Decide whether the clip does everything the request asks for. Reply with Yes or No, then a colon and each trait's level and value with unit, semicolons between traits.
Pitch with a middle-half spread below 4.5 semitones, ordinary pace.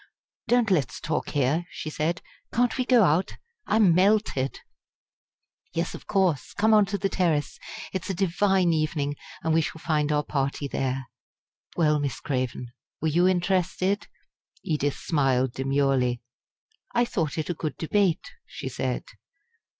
No: average, 5.0 semitones; average, 150 wpm